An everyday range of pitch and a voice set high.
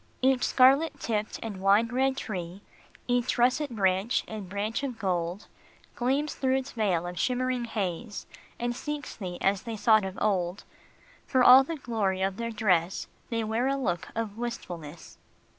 Yes: average, 4.8 semitones; high, 220 Hz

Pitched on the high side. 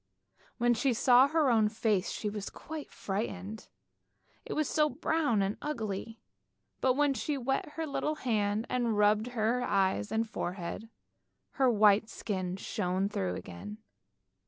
Yes: high, 220 Hz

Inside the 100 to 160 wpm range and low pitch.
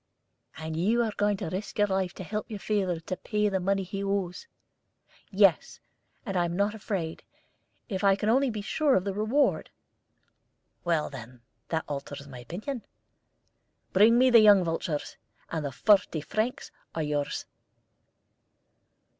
No: average, 155 wpm; high, 195 Hz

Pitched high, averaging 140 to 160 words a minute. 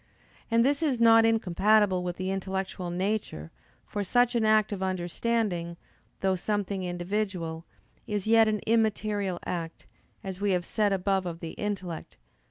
Yes: high, 195 Hz; average, 155 wpm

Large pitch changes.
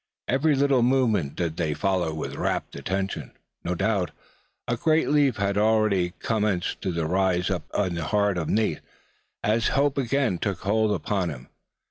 No: average, 4.6 semitones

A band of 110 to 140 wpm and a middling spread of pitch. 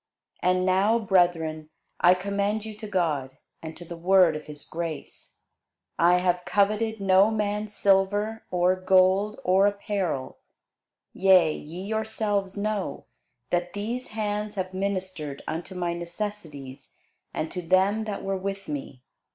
Yes: slow, 135 wpm; average, 3.0 semitones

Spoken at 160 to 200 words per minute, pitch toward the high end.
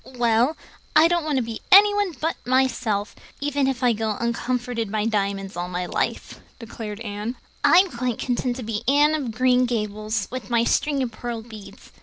Yes: average, 180 wpm; high, 240 Hz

